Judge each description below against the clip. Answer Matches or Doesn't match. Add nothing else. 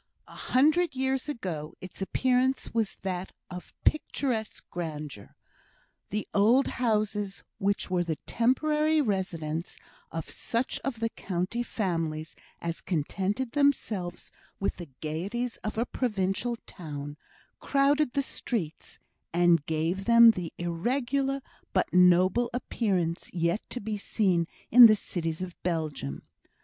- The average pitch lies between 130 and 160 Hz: Doesn't match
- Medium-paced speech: Doesn't match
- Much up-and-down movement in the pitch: Matches